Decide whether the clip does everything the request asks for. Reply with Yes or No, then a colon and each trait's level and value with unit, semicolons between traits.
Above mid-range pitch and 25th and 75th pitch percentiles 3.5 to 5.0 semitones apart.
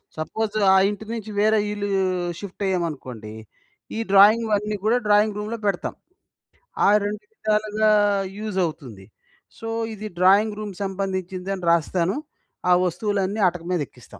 No: high, 200 Hz; average, 2.9 semitones